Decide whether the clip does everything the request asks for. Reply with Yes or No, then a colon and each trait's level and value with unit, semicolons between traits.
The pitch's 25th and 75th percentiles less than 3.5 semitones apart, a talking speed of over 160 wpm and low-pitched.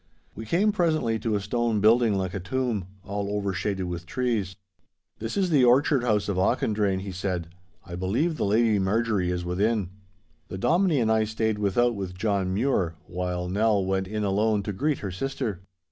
No: average, 3.8 semitones; average, 180 wpm; low, 105 Hz